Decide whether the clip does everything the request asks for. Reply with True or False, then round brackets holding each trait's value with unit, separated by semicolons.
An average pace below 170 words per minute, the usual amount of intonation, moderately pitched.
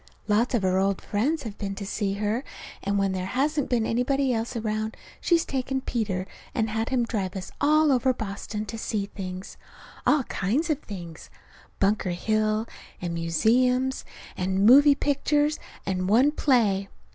False (160 wpm; 4.9 semitones; 220 Hz)